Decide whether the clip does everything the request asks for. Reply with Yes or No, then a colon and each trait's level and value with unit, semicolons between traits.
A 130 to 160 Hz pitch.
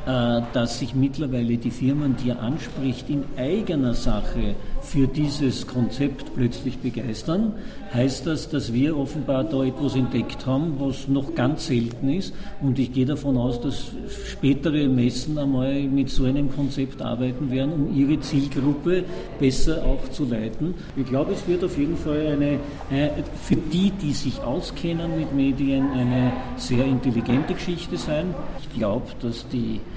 Yes: low, 135 Hz